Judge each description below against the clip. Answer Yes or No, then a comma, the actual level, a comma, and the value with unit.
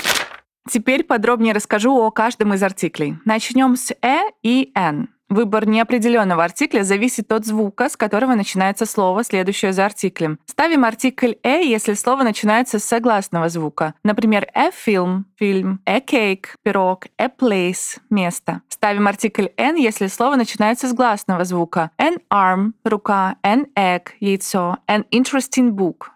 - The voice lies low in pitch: No, high, 215 Hz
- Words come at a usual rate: Yes, average, 140 wpm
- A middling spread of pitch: Yes, average, 4.0 semitones